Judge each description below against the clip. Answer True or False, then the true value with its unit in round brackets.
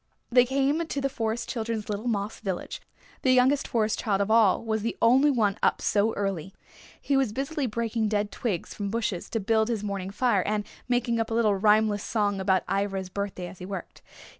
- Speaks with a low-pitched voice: False (220 Hz)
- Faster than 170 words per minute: True (200 wpm)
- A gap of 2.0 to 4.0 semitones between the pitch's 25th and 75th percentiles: True (2.9 semitones)